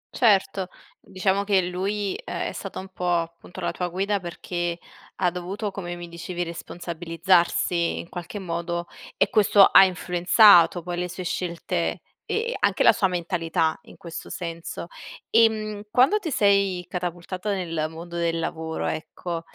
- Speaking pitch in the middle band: Yes, medium, 180 Hz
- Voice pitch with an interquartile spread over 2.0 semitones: Yes, narrow, 2.4 semitones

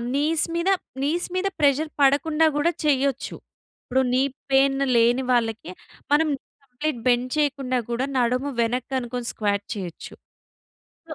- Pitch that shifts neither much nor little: Yes, average, 3.3 semitones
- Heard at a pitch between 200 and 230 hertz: No, very high, 265 Hz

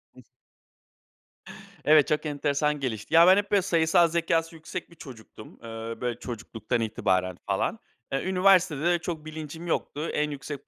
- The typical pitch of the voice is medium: Yes, medium, 150 Hz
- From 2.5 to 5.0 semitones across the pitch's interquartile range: No, wide, 5.4 semitones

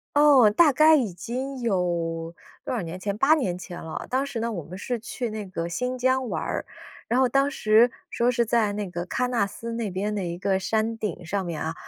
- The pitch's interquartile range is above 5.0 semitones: Yes, wide, 5.4 semitones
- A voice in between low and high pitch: No, high, 215 Hz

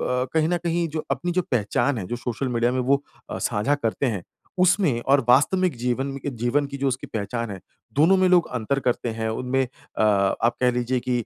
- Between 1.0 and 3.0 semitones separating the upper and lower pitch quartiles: No, average, 3.6 semitones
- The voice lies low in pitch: Yes, low, 130 Hz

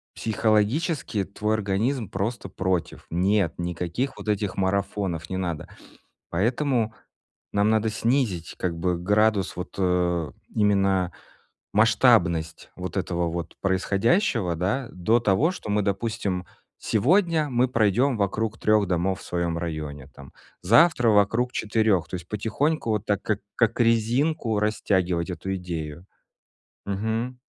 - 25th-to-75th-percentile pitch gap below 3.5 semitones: No, average, 4.1 semitones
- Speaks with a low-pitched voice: Yes, low, 100 Hz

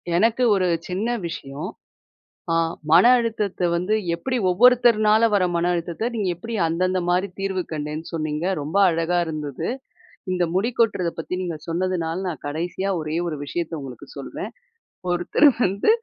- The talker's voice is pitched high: No, medium, 180 Hz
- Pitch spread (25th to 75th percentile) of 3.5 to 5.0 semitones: Yes, average, 3.8 semitones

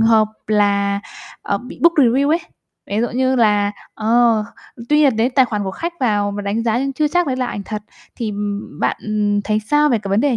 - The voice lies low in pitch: No, high, 225 Hz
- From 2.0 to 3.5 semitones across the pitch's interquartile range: No, average, 4.1 semitones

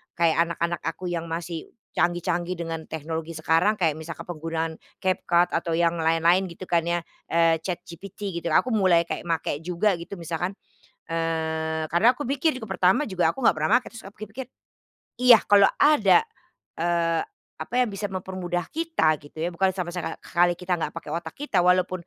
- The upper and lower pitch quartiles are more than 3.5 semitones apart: No, narrow, 2.5 semitones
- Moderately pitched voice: Yes, medium, 175 Hz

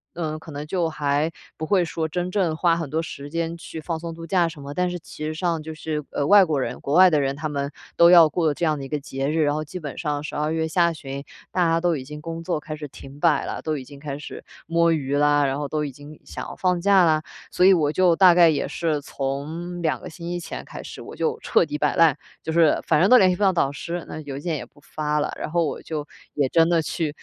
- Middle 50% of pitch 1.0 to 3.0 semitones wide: Yes, narrow, 2.6 semitones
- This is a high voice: No, medium, 160 Hz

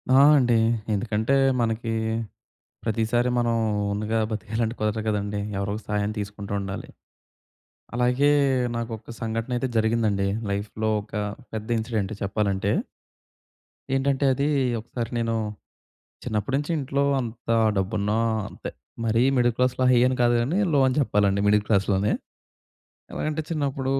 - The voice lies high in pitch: No, low, 115 Hz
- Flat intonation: No, average, 3.0 semitones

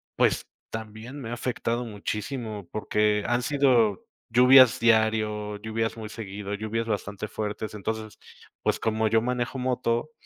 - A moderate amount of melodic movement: No, narrow, 2.2 semitones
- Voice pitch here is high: No, low, 110 Hz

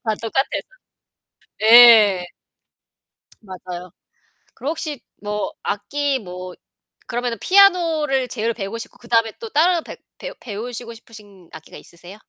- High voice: Yes, high, 230 Hz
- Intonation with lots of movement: No, average, 4.9 semitones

